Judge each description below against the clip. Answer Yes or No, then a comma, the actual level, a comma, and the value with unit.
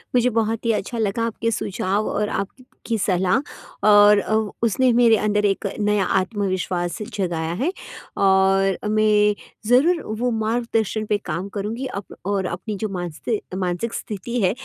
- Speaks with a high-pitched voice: Yes, high, 210 Hz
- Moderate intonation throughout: Yes, average, 3.0 semitones